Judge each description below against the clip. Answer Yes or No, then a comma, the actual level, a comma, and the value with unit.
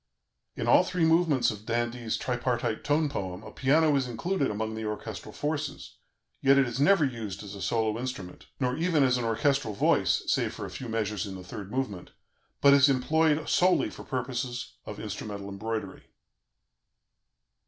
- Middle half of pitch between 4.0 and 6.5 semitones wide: Yes, average, 4.6 semitones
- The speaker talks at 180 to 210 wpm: No, average, 170 wpm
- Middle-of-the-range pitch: No, low, 125 Hz